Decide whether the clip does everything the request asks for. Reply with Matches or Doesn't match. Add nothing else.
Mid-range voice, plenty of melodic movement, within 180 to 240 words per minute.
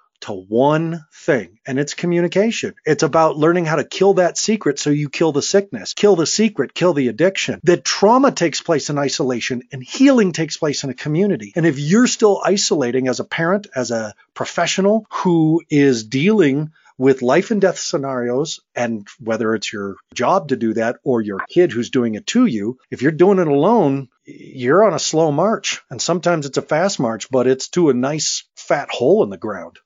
Matches